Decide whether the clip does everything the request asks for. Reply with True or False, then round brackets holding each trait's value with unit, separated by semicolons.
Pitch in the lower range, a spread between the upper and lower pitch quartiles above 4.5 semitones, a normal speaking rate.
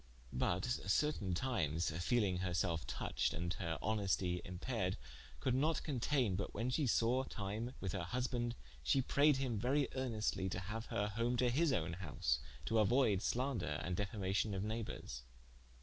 True (105 Hz; 5.6 semitones; 160 wpm)